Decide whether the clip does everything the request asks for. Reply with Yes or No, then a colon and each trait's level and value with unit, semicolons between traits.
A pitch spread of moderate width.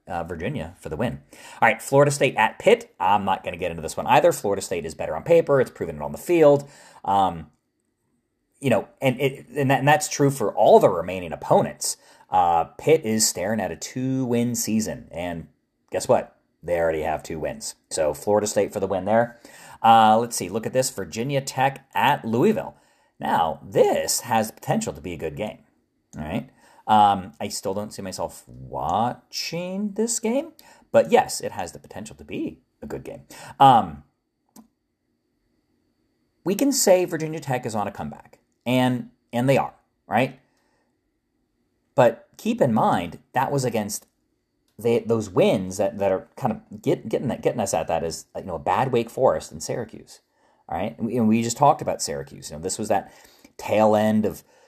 No: wide, 5.9 semitones